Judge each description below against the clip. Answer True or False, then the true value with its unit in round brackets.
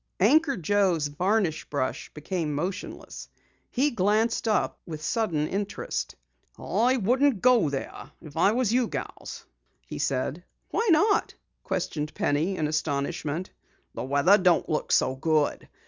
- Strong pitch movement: True (6.7 semitones)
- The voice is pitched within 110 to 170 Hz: False (180 Hz)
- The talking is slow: True (130 wpm)